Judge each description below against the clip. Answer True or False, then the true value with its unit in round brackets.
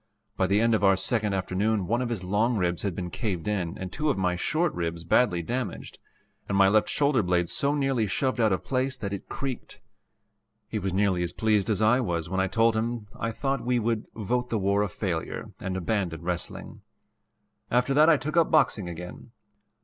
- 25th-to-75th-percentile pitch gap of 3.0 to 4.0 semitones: False (4.7 semitones)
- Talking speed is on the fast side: True (210 wpm)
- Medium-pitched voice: False (105 Hz)